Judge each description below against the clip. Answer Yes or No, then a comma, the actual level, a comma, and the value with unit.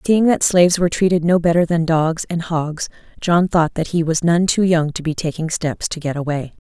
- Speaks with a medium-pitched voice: Yes, medium, 165 Hz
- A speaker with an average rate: No, fast, 235 wpm